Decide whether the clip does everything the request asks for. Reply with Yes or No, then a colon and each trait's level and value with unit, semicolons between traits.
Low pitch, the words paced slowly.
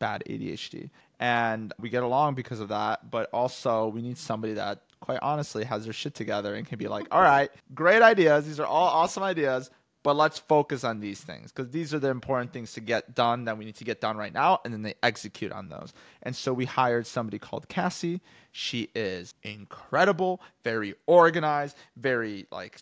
No: low, 125 Hz; fast, 205 wpm